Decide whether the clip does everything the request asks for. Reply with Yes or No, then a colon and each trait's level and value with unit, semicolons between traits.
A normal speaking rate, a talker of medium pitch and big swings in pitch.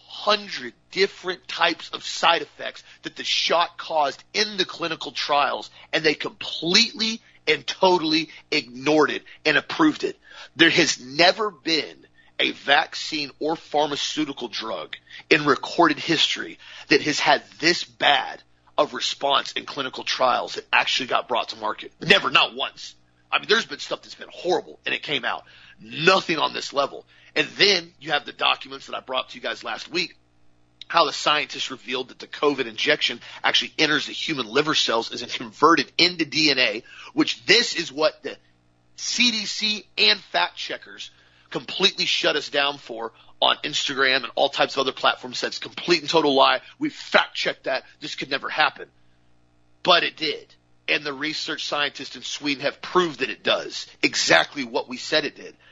Yes: average, 170 wpm; medium, 155 Hz; wide, 7.9 semitones